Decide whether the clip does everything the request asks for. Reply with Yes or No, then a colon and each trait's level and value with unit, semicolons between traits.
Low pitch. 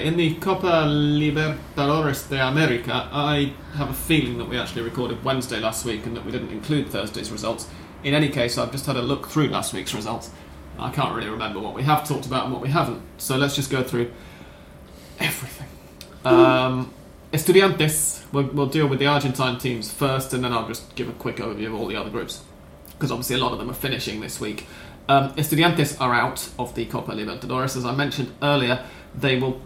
Yes: low, 130 Hz